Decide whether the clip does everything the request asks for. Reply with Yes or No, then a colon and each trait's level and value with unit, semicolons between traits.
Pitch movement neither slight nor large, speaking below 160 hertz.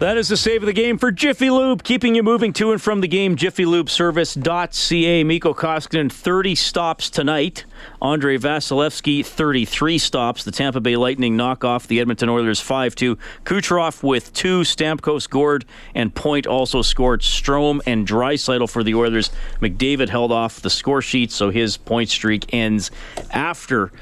No: wide, 6.1 semitones; medium, 140 Hz